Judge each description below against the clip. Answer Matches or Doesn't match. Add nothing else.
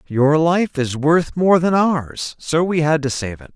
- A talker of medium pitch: Matches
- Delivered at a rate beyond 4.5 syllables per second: Doesn't match